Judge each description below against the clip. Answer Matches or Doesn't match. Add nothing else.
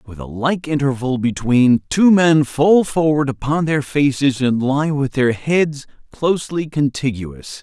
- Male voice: Matches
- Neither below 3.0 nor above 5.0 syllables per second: Matches